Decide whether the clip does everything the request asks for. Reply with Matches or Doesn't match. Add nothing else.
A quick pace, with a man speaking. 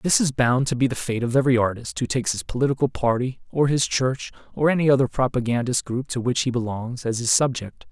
Matches